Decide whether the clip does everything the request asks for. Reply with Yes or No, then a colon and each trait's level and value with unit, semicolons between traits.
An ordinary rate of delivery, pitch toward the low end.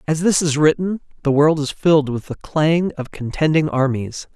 No: average, 195 wpm; medium, 150 Hz